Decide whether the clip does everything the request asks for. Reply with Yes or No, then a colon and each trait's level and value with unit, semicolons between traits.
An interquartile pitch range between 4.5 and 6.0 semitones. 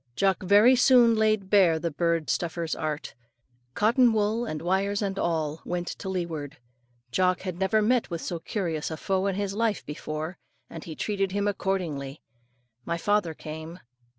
No: average, 4.1 semitones